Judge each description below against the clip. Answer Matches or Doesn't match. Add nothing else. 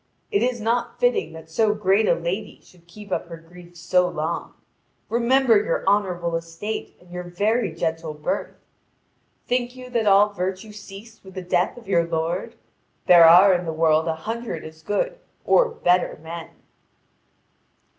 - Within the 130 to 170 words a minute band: Matches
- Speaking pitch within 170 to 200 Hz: Matches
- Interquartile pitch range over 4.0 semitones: Matches